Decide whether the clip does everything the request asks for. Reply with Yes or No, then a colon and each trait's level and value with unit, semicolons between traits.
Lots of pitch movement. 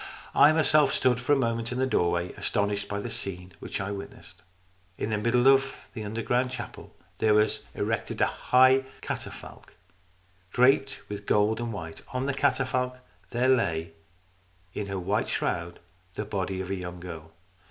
No: average, 4.9 semitones